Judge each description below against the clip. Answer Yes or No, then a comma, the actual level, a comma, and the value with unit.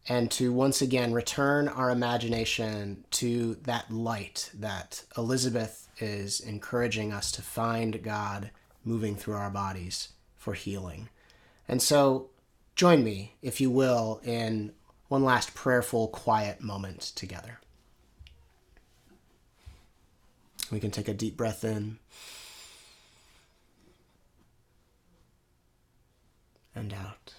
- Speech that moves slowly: Yes, slow, 105 wpm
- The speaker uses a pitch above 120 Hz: No, low, 110 Hz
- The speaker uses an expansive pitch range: No, average, 3.2 semitones